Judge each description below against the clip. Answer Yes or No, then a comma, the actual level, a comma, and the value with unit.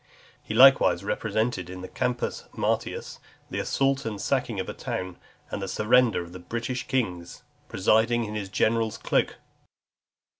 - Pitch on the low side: Yes, low, 110 Hz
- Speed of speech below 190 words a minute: Yes, average, 150 wpm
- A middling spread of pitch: Yes, average, 4.7 semitones